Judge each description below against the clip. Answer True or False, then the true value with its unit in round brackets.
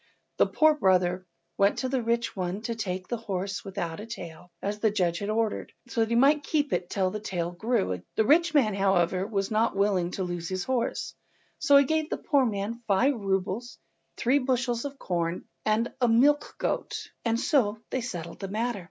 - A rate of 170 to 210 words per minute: True (200 wpm)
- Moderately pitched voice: False (215 Hz)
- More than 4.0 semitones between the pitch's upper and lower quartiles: True (4.5 semitones)